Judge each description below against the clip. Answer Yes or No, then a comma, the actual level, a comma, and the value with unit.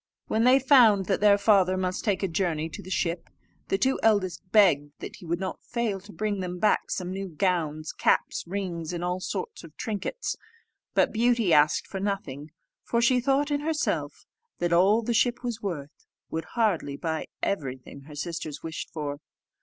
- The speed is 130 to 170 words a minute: No, average, 180 wpm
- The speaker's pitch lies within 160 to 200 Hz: Yes, high, 190 Hz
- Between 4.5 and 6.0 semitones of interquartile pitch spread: Yes, average, 5.0 semitones